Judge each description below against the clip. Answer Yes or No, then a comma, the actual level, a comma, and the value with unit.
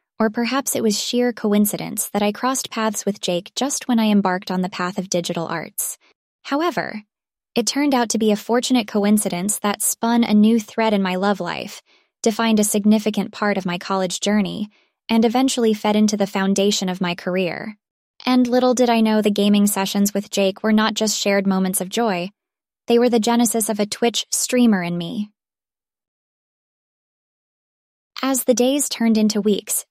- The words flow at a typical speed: Yes, average, 180 wpm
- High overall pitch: Yes, high, 215 Hz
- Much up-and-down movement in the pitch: No, average, 2.9 semitones